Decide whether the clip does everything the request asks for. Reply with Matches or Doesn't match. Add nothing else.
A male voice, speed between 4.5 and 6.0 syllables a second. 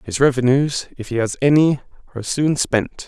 Matches